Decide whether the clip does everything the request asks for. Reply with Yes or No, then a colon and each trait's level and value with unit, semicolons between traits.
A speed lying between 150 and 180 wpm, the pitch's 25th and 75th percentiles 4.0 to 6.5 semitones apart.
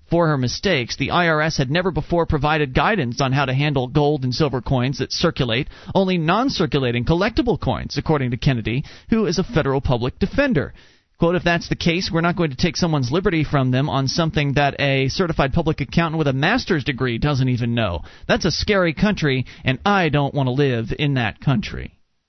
No: average, 200 wpm; average, 4.3 semitones